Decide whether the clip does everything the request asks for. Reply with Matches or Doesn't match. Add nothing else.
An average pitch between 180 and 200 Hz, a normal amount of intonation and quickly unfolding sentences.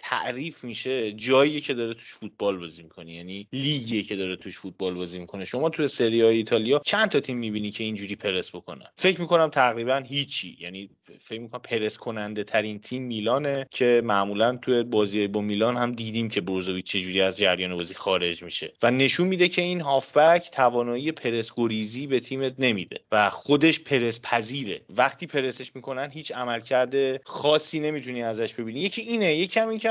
Doesn't match